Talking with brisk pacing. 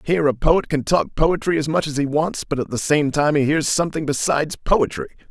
Yes: fast, 240 wpm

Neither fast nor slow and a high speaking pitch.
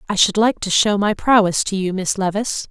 No: fast, 245 wpm; high, 200 Hz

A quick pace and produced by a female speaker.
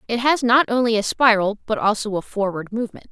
Yes: fast, 210 wpm; female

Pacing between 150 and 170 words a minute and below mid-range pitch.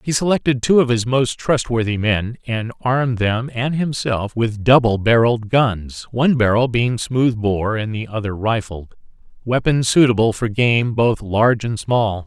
Yes: average, 165 wpm; low, 115 Hz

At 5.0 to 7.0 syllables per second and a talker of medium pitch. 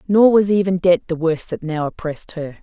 Yes: 5.4 syllables/s; medium, 175 Hz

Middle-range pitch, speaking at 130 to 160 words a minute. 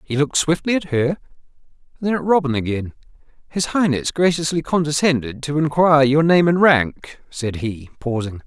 Yes: medium, 145 Hz; average, 155 wpm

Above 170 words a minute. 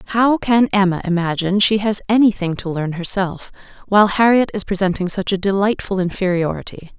No: average, 165 wpm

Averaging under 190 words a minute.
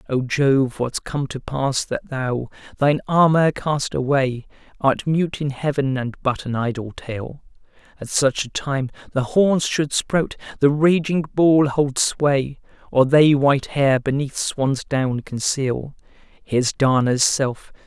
Yes: average, 150 wpm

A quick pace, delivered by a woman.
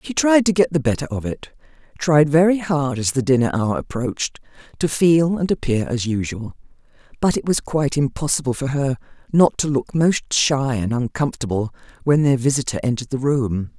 No: average, 185 wpm; female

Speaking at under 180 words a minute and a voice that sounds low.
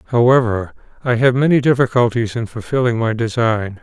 Yes: average, 140 wpm; low, 120 Hz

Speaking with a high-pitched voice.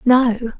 Yes: high, 240 Hz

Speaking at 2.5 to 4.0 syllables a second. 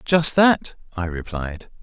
Yes: 3.5 syllables/s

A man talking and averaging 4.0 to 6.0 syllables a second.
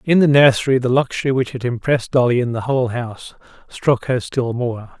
Yes: male; 5.7 syllables/s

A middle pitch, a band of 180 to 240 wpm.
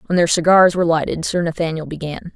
Yes: medium, 165 Hz; fast, 205 wpm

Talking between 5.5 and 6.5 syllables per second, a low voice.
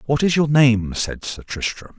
No: 4.3 syllables/s; low, 125 Hz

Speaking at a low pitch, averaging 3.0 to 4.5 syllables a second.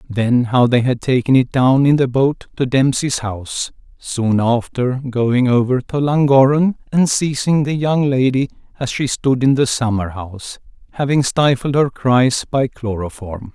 Yes: low, 130 Hz; 4.3 syllables/s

